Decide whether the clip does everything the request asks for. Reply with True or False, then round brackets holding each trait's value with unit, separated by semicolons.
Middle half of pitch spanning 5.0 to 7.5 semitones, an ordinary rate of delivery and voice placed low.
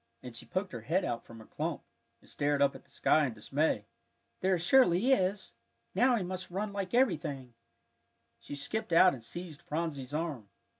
False (5.4 semitones; 190 wpm; 165 Hz)